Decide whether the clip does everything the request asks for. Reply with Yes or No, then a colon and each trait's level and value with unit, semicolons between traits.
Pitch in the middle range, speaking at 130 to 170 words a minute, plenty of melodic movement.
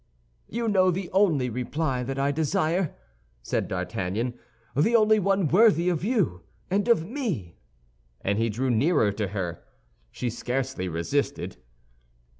Yes: medium, 145 Hz; slow, 135 wpm; wide, 9.0 semitones